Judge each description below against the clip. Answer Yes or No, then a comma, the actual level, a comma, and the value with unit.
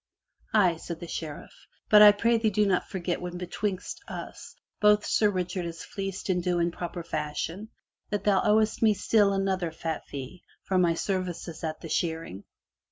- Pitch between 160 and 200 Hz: Yes, medium, 185 Hz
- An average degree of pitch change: Yes, average, 3.4 semitones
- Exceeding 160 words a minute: Yes, average, 175 wpm